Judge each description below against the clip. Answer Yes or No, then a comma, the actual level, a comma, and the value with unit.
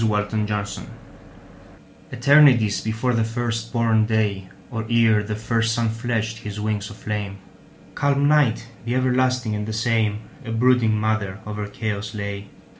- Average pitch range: No, narrow, 1.9 semitones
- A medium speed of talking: No, slow, 130 wpm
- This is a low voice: Yes, low, 110 Hz